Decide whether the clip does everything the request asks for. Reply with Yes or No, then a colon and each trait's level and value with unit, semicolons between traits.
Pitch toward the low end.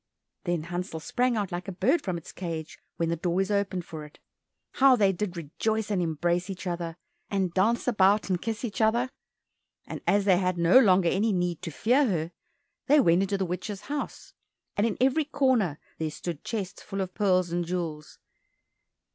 No: medium, 185 Hz